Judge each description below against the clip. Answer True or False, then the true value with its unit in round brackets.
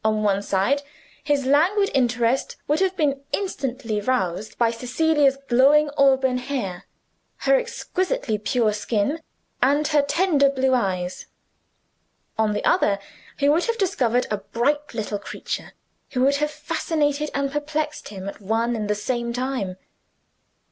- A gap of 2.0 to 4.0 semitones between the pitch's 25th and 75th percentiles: False (5.2 semitones)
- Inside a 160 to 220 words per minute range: False (140 wpm)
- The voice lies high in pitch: True (265 Hz)